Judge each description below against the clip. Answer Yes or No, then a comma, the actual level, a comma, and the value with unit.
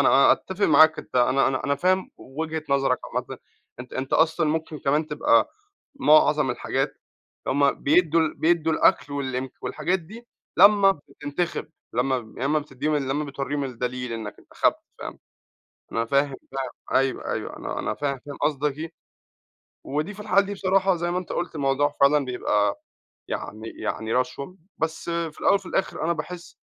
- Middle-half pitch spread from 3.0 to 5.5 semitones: Yes, average, 3.9 semitones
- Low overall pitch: No, medium, 145 Hz